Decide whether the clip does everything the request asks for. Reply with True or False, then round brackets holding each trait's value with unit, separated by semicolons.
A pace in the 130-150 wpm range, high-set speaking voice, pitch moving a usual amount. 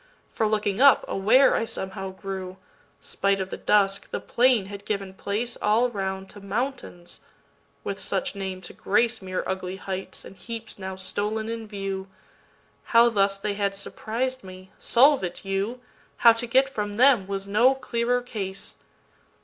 True (140 wpm; 205 Hz; 3.5 semitones)